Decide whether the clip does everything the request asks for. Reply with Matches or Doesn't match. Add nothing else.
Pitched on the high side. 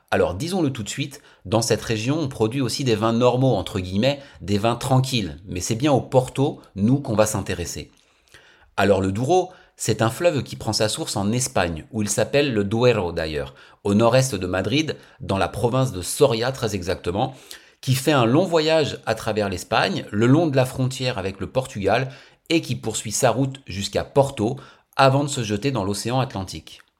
Doesn't match